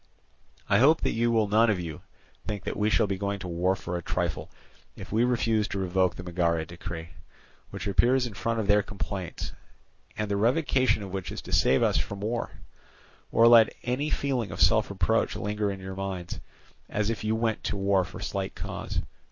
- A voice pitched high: No, low, 100 Hz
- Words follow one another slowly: No, average, 200 wpm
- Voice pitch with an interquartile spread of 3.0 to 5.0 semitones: Yes, average, 3.4 semitones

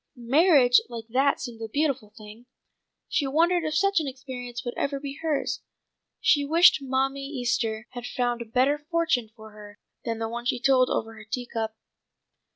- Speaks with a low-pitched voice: No, very high, 255 Hz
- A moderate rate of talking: Yes, average, 175 wpm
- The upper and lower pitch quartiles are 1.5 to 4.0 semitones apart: Yes, average, 3.6 semitones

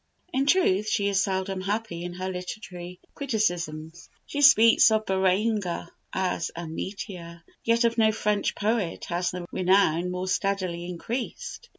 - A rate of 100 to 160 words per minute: Yes, average, 145 wpm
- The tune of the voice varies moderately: Yes, average, 3.6 semitones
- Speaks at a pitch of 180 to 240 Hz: Yes, high, 190 Hz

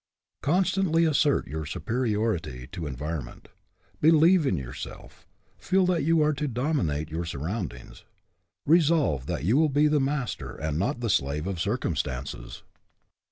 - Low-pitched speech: Yes, low, 115 Hz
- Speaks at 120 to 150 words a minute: Yes, average, 140 wpm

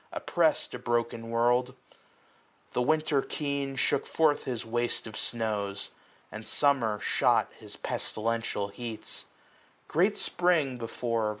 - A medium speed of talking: No, slow, 115 wpm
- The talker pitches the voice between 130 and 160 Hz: No, low, 120 Hz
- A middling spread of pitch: Yes, average, 3.6 semitones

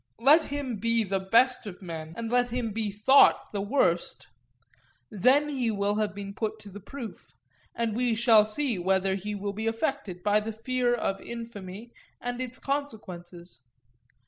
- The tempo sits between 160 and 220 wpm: Yes, average, 170 wpm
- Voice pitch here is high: Yes, high, 220 Hz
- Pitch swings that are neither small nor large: Yes, average, 3.6 semitones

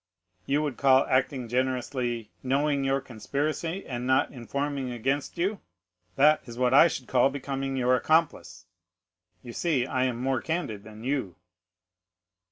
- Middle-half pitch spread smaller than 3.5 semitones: Yes, narrow, 2.5 semitones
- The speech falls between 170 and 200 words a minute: No, average, 145 wpm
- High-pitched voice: No, low, 130 Hz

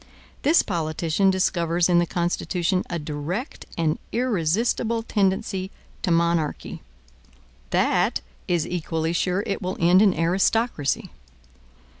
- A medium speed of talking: No, slow, 110 wpm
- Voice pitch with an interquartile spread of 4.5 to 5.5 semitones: No, average, 2.8 semitones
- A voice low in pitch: No, medium, 175 Hz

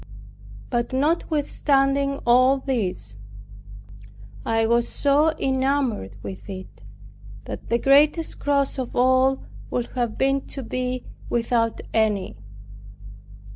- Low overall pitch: No, very high, 260 Hz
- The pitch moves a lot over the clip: No, average, 3.0 semitones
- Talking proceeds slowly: Yes, slow, 100 wpm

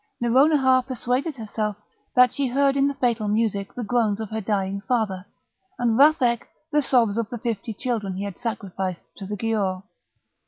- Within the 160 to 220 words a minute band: Yes, average, 170 wpm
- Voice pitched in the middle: No, high, 230 Hz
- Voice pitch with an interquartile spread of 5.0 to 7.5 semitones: No, average, 3.8 semitones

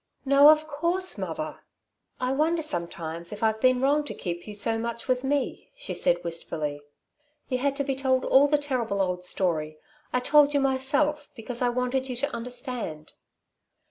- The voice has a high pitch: Yes, very high, 255 Hz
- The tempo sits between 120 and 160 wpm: No, average, 175 wpm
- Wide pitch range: Yes, wide, 5.7 semitones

